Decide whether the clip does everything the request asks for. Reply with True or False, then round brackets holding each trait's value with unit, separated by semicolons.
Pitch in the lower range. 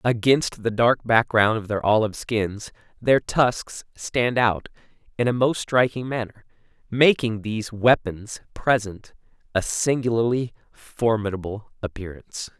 True (115 Hz)